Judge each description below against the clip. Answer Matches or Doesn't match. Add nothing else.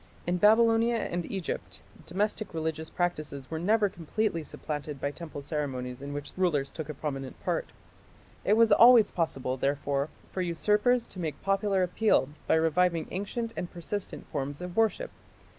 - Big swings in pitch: Matches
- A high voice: Doesn't match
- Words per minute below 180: Matches